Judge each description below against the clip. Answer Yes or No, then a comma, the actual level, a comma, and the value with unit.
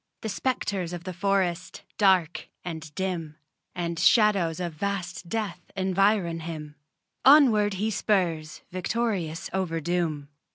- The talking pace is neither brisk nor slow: No, slow, 120 wpm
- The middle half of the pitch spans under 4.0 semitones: Yes, average, 3.3 semitones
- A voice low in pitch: No, medium, 180 Hz